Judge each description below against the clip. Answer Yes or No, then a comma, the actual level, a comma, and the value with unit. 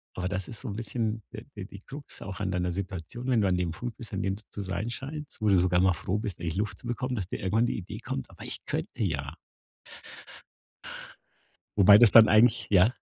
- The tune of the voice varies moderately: Yes, average, 4.0 semitones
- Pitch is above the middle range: No, low, 100 Hz